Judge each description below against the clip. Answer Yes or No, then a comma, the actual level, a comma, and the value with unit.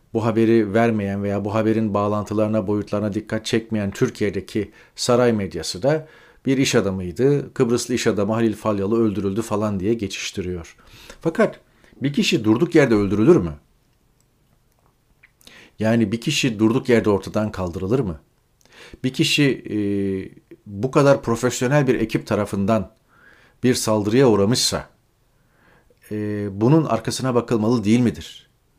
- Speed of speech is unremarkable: Yes, average, 125 wpm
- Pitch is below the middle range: Yes, low, 115 Hz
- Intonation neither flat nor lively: Yes, average, 3.4 semitones